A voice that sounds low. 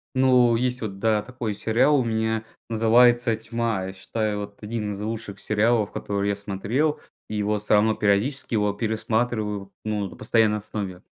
Yes: low, 110 Hz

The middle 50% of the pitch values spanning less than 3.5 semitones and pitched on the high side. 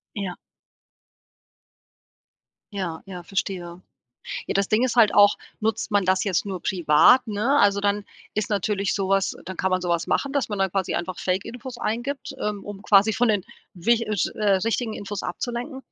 Yes: average, 2.9 semitones; high, 205 Hz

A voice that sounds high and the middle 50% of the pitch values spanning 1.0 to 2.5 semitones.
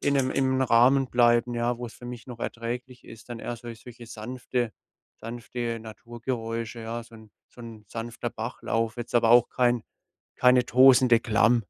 No: low, 120 Hz; narrow, 1.3 semitones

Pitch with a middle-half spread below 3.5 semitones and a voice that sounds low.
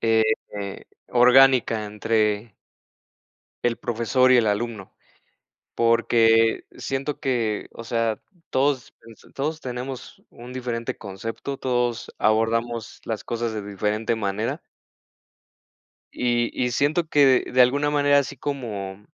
Yes: narrow, 2.6 semitones; low, 120 Hz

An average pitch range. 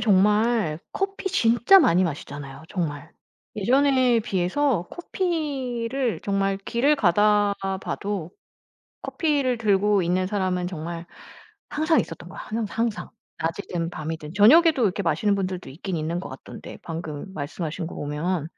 No: wide, 5.9 semitones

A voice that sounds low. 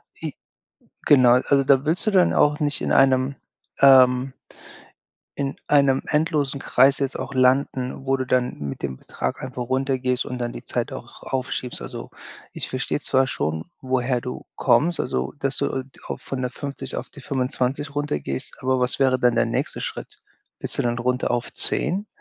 Yes: low, 130 Hz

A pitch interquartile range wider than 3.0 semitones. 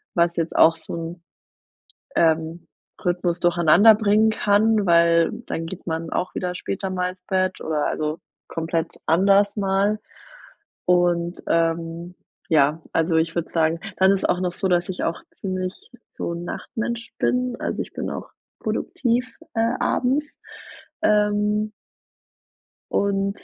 Yes: average, 3.6 semitones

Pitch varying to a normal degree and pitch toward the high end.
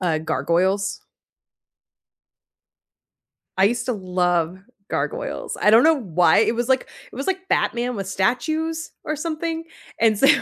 No: wide, 8.8 semitones; high, 230 Hz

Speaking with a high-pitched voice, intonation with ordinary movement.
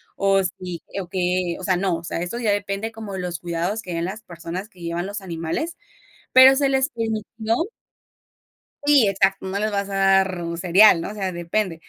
Yes: high, 195 Hz; average, 3.5 semitones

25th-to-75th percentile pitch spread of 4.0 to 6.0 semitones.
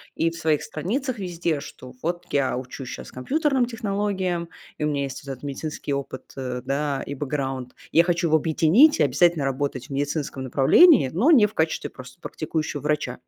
Yes: average, 4.4 semitones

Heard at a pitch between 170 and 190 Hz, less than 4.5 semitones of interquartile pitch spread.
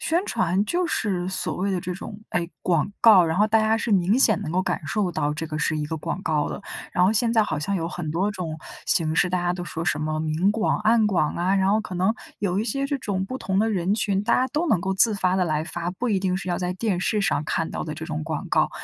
Yes: medium, 185 Hz; average, 4.0 semitones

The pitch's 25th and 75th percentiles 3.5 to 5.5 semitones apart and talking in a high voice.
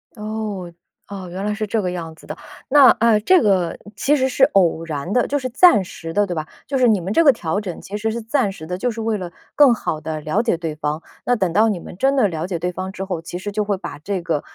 Yes: average, 4.6 semitones; high, 200 Hz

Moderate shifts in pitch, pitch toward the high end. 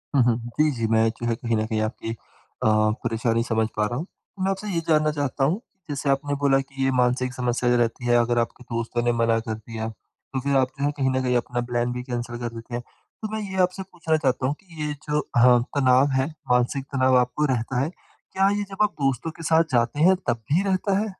No: average, 4.2 semitones; low, 130 Hz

